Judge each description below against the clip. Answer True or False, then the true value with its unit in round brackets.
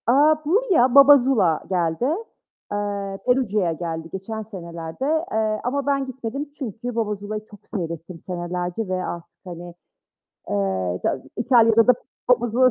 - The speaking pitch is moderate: False (215 Hz)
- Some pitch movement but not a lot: False (6.2 semitones)